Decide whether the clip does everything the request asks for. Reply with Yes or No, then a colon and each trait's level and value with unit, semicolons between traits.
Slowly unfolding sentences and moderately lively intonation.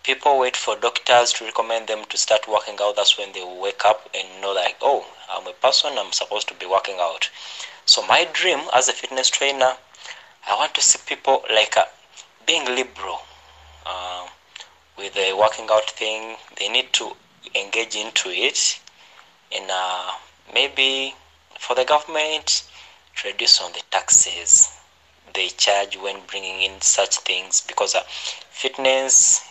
No: average, 155 wpm; average, 4.9 semitones